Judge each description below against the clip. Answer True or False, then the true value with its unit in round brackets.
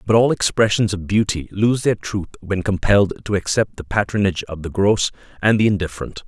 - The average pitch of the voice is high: False (100 Hz)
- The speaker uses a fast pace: False (190 wpm)